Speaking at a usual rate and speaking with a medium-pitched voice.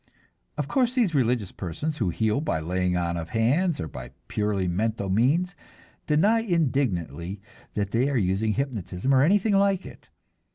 No: average, 160 wpm; low, 115 Hz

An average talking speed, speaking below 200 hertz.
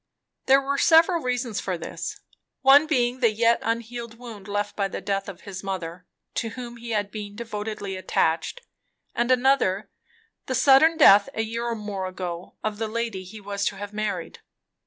No: average, 180 wpm; high, 220 Hz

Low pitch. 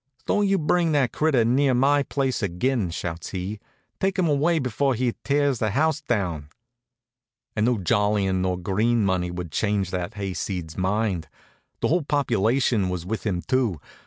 Yes: low, 110 Hz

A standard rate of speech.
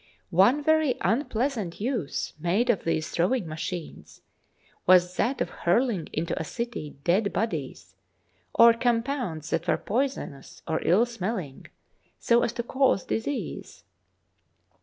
No: slow, 130 wpm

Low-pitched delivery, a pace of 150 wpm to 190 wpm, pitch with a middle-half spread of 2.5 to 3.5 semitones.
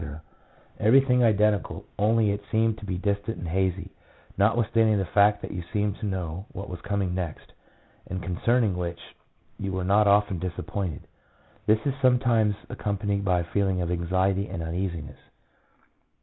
Yes: low, 100 Hz; average, 155 wpm; average, 2.8 semitones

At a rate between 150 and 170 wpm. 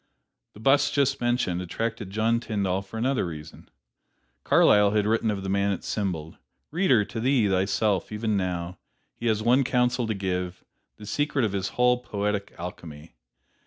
Yes: average, 160 wpm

